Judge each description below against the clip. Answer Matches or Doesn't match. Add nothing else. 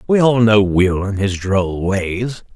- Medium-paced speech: Matches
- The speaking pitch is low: Matches